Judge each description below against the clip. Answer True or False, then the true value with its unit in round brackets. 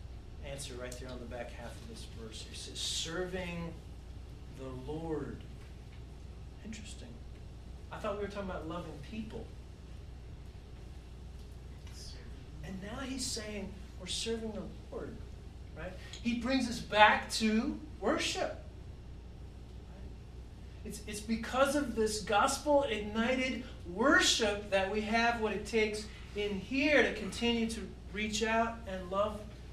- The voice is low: False (210 Hz)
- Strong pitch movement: True (8.7 semitones)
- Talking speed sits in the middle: False (125 wpm)